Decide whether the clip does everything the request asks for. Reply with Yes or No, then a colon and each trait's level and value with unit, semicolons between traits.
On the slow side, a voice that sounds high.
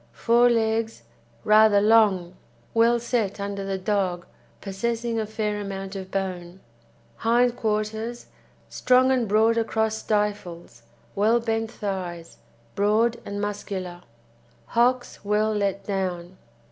Yes: slow, 115 wpm; high, 210 Hz